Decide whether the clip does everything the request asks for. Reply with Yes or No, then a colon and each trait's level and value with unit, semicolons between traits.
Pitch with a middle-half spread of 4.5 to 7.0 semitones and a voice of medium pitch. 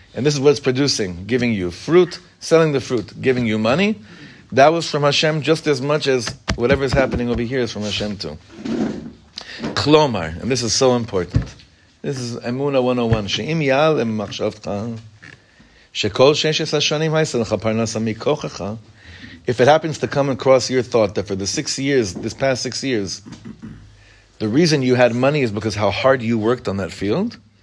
No: average, 4.8 semitones; low, 125 Hz